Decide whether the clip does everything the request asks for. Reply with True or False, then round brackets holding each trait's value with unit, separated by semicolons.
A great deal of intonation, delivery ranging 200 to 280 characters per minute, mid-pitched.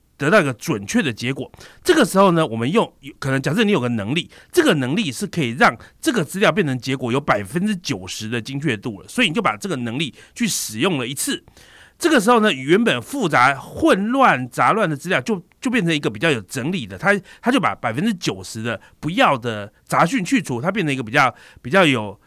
False (8.7 semitones; 330 characters per minute; 160 Hz)